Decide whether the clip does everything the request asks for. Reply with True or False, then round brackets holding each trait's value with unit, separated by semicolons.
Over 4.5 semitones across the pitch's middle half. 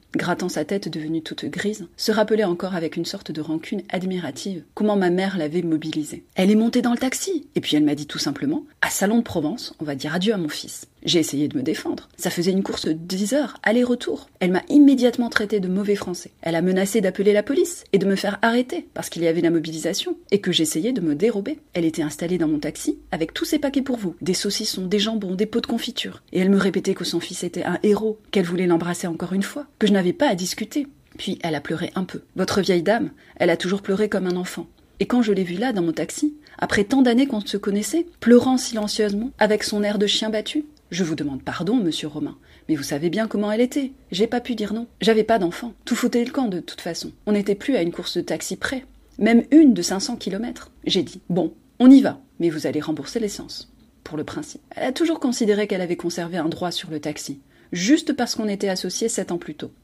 True (5.3 semitones)